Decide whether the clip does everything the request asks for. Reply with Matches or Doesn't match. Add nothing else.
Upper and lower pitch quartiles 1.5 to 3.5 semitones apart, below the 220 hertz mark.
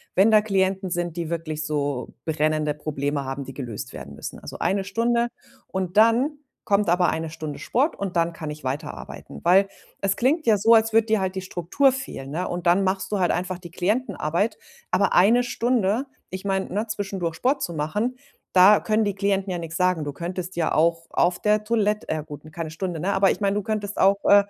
Doesn't match